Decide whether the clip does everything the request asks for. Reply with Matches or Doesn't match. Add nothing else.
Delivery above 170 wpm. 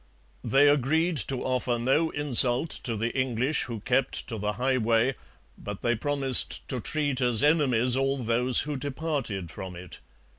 Doesn't match